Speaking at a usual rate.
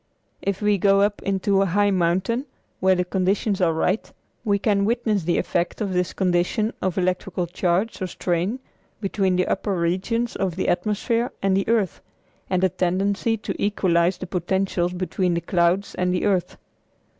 Yes: average, 170 wpm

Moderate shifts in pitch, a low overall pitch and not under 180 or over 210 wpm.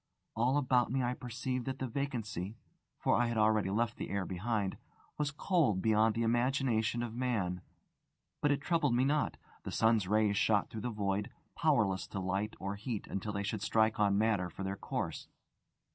Yes: average, 3.7 semitones; low, 110 Hz; average, 185 wpm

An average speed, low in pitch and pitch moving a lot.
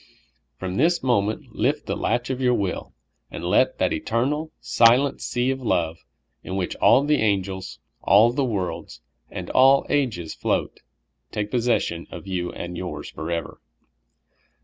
Yes: average, 150 wpm; low, 110 Hz; wide, 6.0 semitones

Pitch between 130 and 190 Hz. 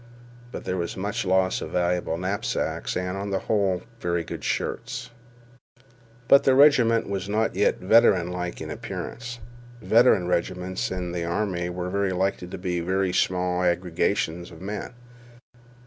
No: very low, 95 Hz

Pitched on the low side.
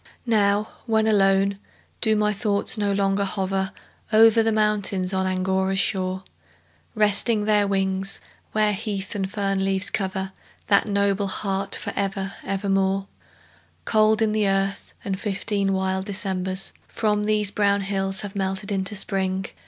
No: high, 200 Hz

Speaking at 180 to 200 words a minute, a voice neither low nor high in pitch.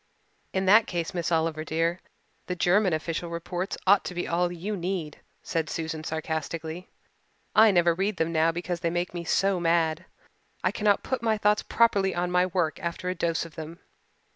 Yes: average, 185 wpm; medium, 175 Hz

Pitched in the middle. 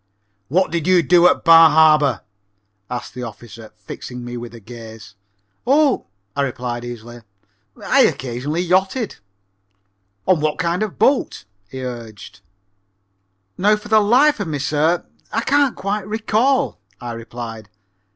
Yes: medium, 155 Hz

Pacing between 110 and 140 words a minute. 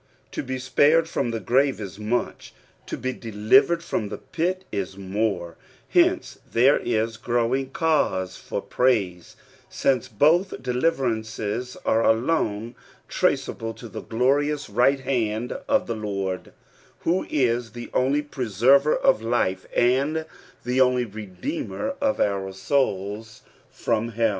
Yes: slow, 135 wpm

